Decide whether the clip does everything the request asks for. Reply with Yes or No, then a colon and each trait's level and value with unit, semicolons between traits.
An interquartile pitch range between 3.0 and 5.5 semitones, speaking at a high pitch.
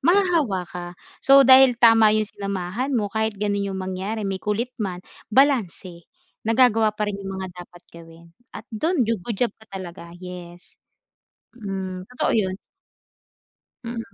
Yes: average, 4.0 semitones; high, 210 Hz